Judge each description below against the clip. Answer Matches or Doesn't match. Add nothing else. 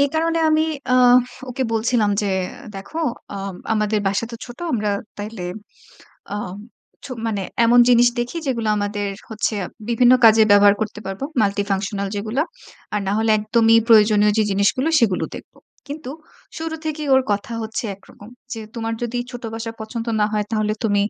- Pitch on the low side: Doesn't match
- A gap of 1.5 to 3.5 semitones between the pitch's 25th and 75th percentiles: Matches